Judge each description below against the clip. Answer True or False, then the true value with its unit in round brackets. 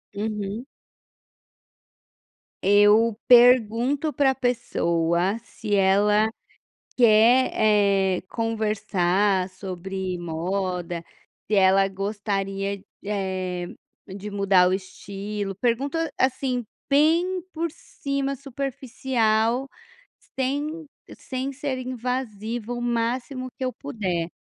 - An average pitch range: True (4.7 semitones)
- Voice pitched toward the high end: True (215 Hz)